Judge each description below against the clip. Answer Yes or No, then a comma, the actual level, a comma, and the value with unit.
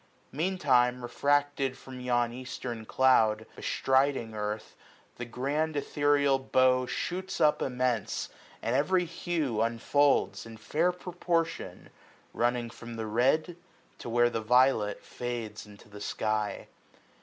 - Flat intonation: No, average, 4.0 semitones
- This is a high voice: No, low, 125 Hz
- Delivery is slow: Yes, slow, 125 wpm